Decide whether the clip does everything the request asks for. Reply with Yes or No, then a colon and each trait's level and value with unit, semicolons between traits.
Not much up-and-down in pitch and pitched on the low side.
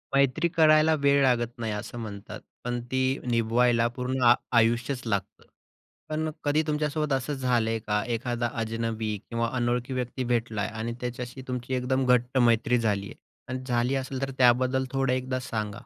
Yes: narrow, 2.3 semitones; low, 125 Hz